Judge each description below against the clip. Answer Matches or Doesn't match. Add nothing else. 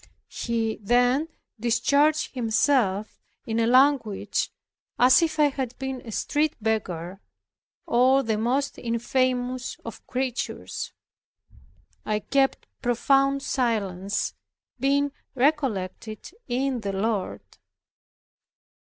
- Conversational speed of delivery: Doesn't match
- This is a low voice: Doesn't match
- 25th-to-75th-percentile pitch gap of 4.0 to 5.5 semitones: Doesn't match